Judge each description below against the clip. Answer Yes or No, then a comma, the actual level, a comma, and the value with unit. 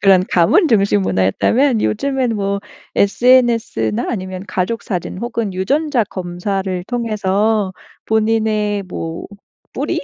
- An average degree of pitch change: Yes, average, 3.8 semitones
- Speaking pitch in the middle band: No, high, 205 Hz